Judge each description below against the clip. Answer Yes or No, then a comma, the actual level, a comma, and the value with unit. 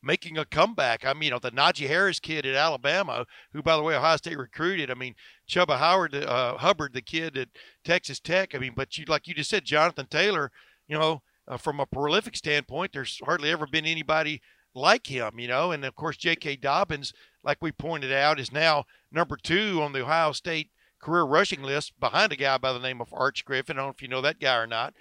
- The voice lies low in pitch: No, medium, 150 Hz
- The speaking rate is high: Yes, fast, 230 wpm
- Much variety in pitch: No, average, 3.2 semitones